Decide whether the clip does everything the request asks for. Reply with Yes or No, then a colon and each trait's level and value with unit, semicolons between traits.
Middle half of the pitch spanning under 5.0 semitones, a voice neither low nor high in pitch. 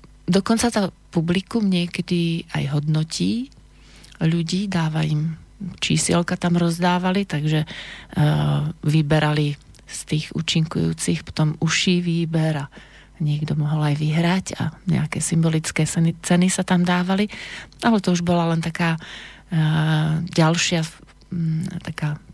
Yes: narrow, 2.4 semitones; medium, 165 Hz